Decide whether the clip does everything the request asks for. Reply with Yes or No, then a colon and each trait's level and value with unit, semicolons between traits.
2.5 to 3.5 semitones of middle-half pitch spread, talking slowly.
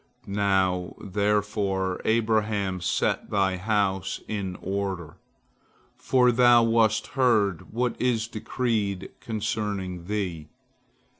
Yes: average, 2.8 semitones; slow, 90 wpm